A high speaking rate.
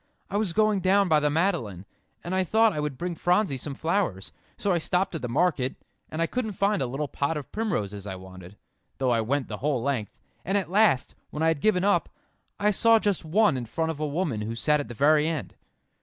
Yes: fast, 230 wpm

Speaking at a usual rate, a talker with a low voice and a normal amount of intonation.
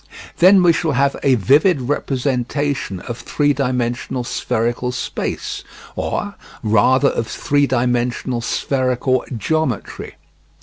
No: slow, 105 wpm; low, 130 Hz; average, 3.0 semitones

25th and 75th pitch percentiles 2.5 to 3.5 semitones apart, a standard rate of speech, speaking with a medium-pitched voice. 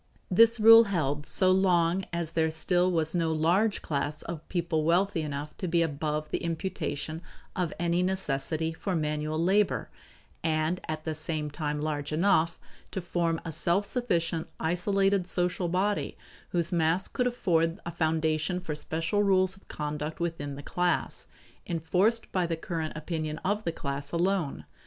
Yes: average, 2.9 semitones; average, 155 wpm; medium, 165 Hz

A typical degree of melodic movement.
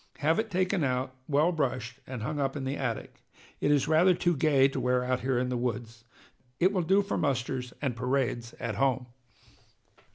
Yes: average, 3.8 semitones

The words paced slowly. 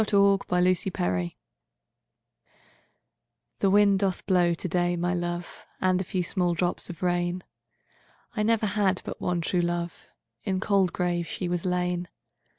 Yes: slow, 130 wpm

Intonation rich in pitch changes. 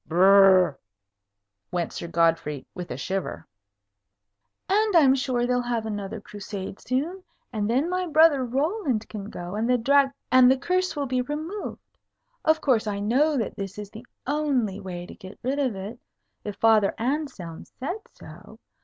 Yes: wide, 6.3 semitones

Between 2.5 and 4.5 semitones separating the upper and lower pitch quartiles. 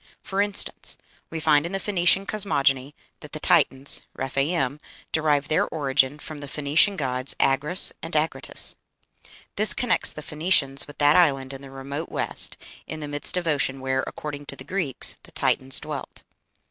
Yes: average, 3.3 semitones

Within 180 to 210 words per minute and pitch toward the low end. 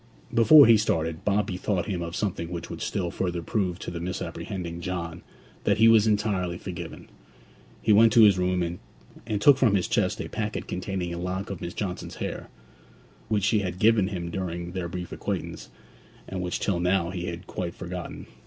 Yes: average, 190 wpm; very low, 90 Hz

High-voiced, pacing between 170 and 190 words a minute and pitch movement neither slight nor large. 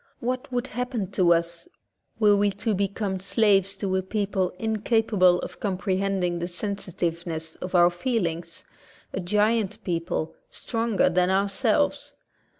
No: high, 195 Hz; slow, 135 wpm; average, 3.3 semitones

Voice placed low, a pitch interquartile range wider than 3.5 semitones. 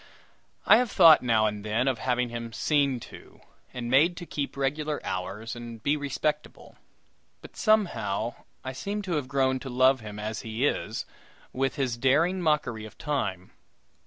Yes: low, 130 Hz; average, 4.6 semitones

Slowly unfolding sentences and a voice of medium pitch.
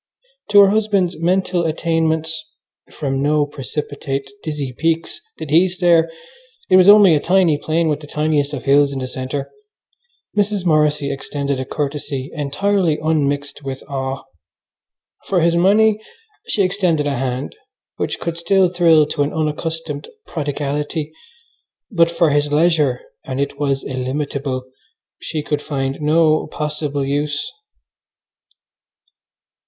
Yes: slow, 130 wpm; medium, 150 Hz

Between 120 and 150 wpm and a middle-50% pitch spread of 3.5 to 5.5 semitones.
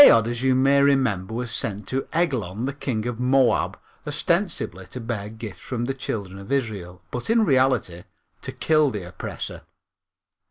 No: average, 165 wpm; average, 4.6 semitones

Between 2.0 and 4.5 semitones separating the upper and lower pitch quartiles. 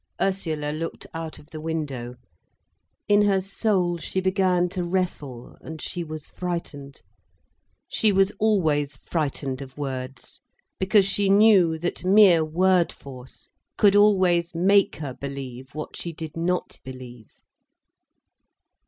No: average, 4.9 semitones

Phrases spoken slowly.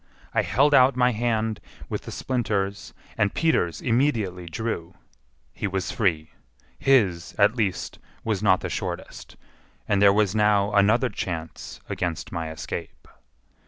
Yes: slow, 130 wpm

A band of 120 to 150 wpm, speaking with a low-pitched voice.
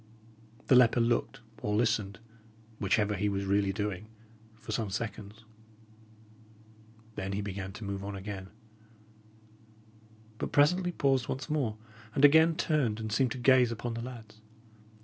Yes: average, 140 wpm; low, 110 Hz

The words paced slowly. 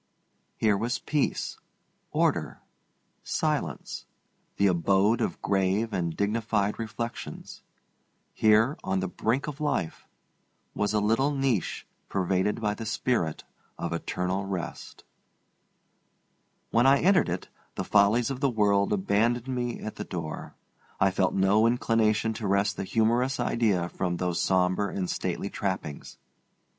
Yes: slow, 130 wpm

